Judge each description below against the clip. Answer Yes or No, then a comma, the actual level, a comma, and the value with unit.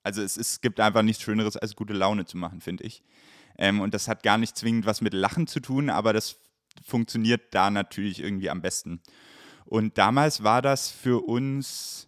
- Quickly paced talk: Yes, fast, 205 wpm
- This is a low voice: Yes, low, 110 Hz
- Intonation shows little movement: No, average, 3.2 semitones